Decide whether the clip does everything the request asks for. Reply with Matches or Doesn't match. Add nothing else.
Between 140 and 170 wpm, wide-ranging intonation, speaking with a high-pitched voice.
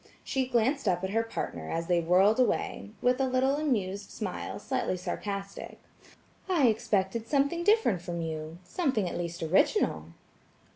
Matches